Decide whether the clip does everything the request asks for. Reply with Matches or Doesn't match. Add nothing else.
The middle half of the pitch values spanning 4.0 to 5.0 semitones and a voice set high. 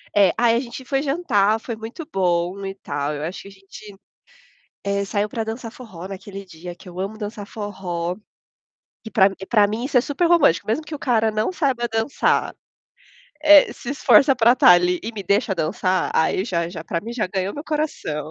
Matches